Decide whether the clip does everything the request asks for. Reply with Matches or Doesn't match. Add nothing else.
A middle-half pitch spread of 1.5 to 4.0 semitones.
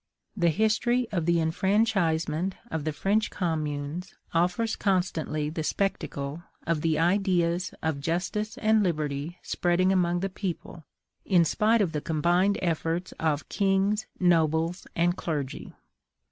Matches